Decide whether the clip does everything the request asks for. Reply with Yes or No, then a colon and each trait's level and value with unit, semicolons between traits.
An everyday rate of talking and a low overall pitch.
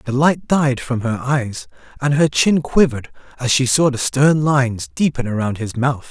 Yes: average, 195 wpm; low, 130 Hz